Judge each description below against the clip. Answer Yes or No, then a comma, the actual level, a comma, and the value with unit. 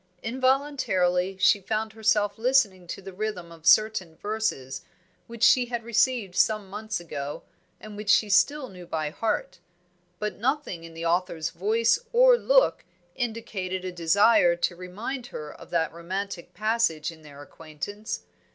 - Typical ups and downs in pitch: Yes, average, 4.7 semitones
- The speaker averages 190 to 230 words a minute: No, average, 150 wpm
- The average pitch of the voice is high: Yes, high, 200 Hz